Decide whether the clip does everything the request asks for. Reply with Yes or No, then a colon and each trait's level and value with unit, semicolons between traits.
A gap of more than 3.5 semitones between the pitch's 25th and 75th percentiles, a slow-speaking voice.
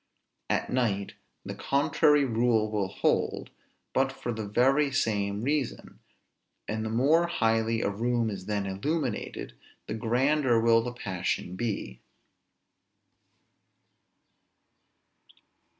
Yes: average, 4.1 semitones; slow, 105 wpm